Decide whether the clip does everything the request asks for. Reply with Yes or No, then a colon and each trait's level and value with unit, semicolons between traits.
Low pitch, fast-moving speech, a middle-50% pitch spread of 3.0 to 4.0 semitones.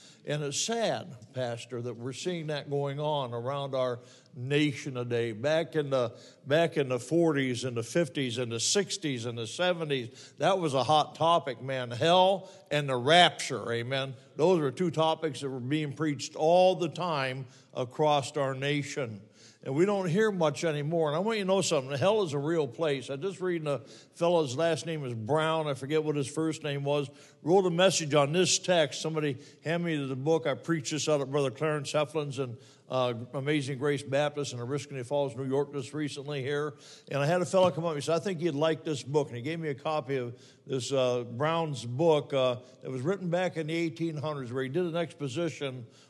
No: medium, 145 Hz; fast, 210 wpm; average, 3.5 semitones